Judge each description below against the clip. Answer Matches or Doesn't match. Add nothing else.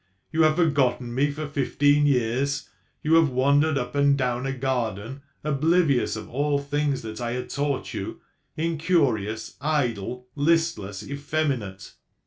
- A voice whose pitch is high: Doesn't match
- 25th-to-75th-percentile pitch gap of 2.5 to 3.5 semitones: Matches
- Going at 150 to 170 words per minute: Doesn't match